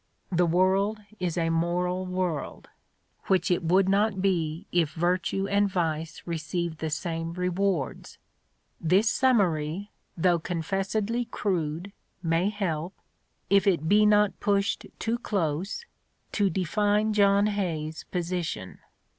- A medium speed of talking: No, slow, 120 wpm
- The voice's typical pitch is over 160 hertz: Yes, medium, 185 Hz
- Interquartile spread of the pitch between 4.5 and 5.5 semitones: No, average, 3.4 semitones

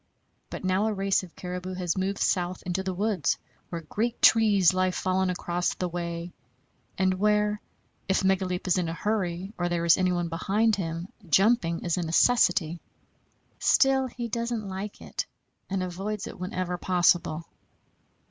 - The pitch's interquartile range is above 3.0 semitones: No, average, 2.7 semitones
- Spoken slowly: No, average, 155 wpm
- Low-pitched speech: No, medium, 185 Hz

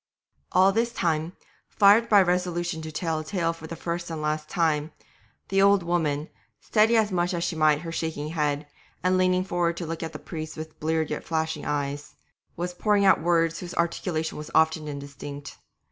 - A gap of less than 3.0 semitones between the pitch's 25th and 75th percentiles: Yes, narrow, 2.6 semitones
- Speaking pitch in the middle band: Yes, medium, 165 Hz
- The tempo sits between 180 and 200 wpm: Yes, average, 190 wpm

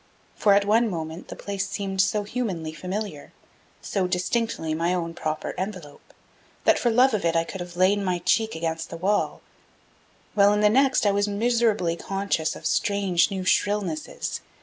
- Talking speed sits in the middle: Yes, average, 170 wpm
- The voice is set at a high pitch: Yes, high, 195 Hz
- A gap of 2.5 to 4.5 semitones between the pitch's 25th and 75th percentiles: Yes, average, 3.5 semitones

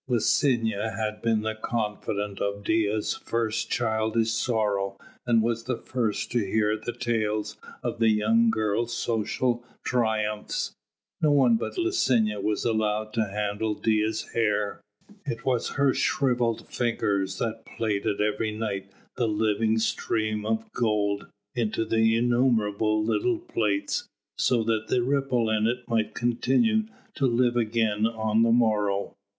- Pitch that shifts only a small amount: Yes, narrow, 1.9 semitones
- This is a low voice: Yes, low, 110 Hz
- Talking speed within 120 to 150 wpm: Yes, slow, 135 wpm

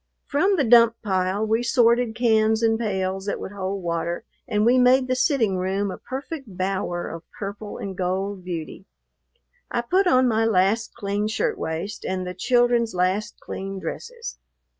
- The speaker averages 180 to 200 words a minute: No, average, 165 wpm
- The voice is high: Yes, high, 215 Hz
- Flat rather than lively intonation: No, average, 4.2 semitones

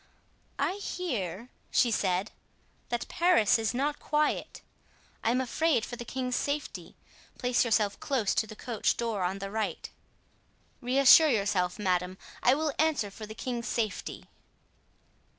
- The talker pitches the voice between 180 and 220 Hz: No, high, 235 Hz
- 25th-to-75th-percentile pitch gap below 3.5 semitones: No, average, 4.7 semitones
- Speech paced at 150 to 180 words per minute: No, average, 140 wpm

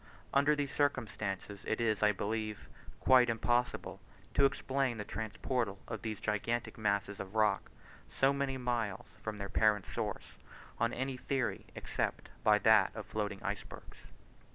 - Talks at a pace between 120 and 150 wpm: Yes, average, 145 wpm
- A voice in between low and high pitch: No, low, 110 Hz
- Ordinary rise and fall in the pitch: Yes, average, 3.5 semitones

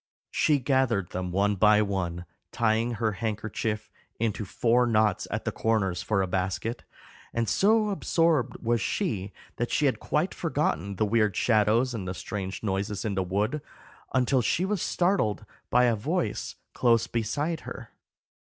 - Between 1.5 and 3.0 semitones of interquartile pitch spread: No, average, 3.9 semitones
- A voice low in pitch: Yes, low, 110 Hz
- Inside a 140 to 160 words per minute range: Yes, average, 155 wpm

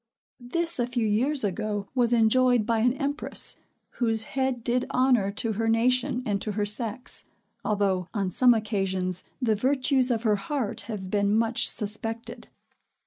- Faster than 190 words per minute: No, average, 155 wpm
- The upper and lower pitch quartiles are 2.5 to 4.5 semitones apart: Yes, average, 3.3 semitones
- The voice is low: No, high, 225 Hz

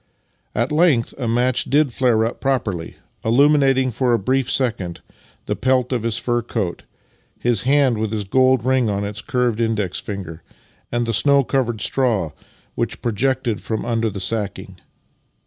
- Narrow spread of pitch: No, average, 3.6 semitones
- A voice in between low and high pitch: No, low, 120 Hz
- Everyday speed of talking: Yes, average, 160 wpm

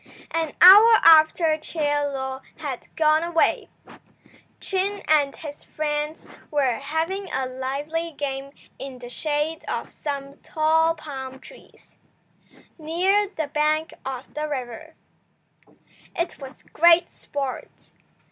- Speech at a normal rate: No, slow, 115 wpm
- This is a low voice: No, very high, 305 Hz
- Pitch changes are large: No, average, 2.9 semitones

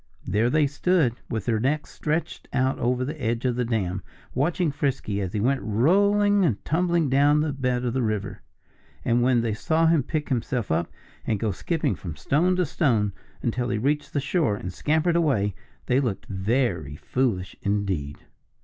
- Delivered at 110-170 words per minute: No, average, 185 wpm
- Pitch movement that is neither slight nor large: No, wide, 6.2 semitones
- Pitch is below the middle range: Yes, low, 125 Hz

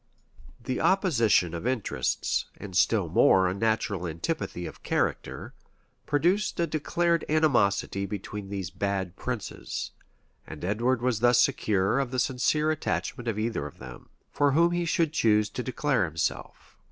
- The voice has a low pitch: Yes, low, 120 Hz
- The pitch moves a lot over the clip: Yes, wide, 7.0 semitones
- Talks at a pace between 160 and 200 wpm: No, average, 145 wpm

